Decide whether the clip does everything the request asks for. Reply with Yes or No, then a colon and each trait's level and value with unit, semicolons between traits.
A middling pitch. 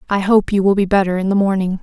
No: high, 195 Hz